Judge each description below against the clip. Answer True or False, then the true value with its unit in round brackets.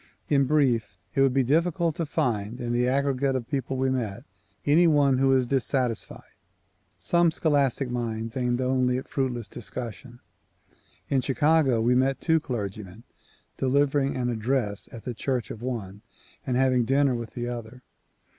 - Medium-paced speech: True (165 wpm)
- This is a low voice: True (130 Hz)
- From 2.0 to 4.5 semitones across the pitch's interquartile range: True (2.5 semitones)